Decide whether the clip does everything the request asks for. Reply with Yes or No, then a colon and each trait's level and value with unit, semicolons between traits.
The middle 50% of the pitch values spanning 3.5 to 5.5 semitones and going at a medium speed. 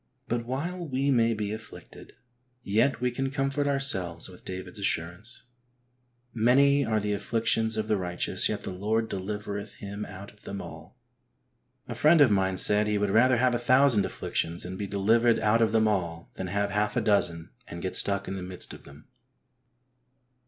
Yes: average, 3.9 semitones; average, 185 wpm